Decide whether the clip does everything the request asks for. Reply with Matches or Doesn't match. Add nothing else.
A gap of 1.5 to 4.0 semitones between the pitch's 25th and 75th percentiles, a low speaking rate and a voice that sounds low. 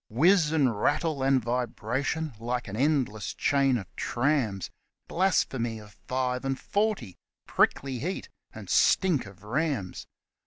Doesn't match